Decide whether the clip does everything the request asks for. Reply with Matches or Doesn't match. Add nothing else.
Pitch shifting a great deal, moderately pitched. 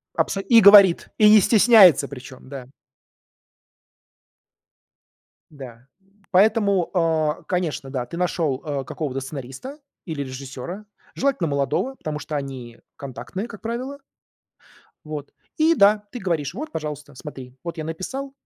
Matches